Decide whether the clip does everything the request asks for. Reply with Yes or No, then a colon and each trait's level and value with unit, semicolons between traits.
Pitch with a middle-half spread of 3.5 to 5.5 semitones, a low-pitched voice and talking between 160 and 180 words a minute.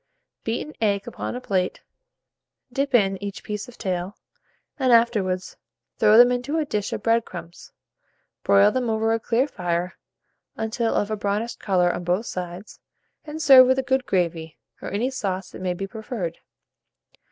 No: average, 4.7 semitones; high, 210 Hz; average, 170 wpm